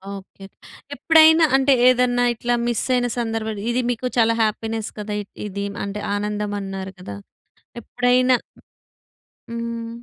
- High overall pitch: Yes, high, 230 Hz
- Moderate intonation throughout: Yes, average, 3.0 semitones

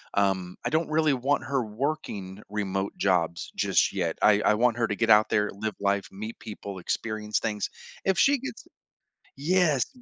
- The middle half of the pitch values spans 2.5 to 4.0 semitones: No, wide, 5.6 semitones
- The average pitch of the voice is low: Yes, low, 110 Hz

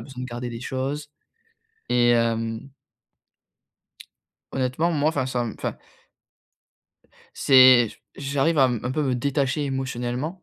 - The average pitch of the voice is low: Yes, low, 130 Hz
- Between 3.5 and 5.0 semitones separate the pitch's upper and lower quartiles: No, average, 2.7 semitones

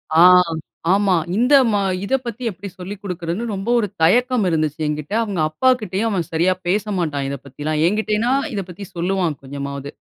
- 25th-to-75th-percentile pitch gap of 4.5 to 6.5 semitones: Yes, average, 5.1 semitones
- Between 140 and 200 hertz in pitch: Yes, medium, 185 Hz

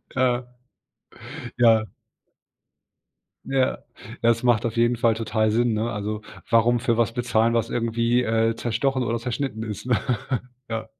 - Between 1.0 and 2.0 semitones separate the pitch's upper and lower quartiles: Yes, narrow, 1.4 semitones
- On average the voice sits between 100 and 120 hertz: Yes, low, 115 Hz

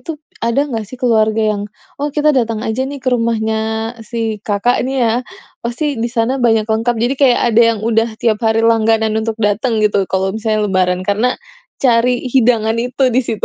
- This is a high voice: Yes, high, 225 Hz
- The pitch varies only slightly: Yes, narrow, 2.2 semitones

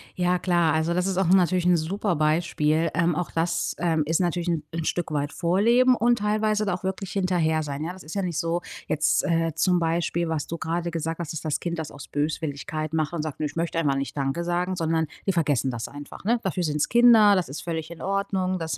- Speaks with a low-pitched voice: No, medium, 170 Hz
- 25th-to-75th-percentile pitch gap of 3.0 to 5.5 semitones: No, narrow, 2.6 semitones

